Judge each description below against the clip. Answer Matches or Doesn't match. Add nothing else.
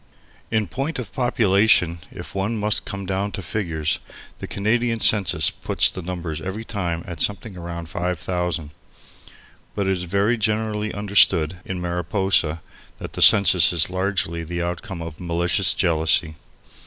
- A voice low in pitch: Matches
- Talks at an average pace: Matches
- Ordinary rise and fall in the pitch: Matches